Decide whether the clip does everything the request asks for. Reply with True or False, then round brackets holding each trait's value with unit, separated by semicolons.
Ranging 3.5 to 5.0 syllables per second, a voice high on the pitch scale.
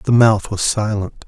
False (4.1 syllables/s; 105 Hz)